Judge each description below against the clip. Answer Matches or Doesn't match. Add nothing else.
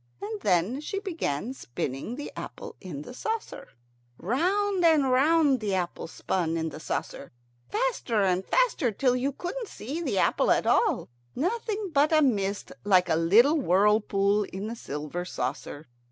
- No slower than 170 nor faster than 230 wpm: Doesn't match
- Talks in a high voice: Matches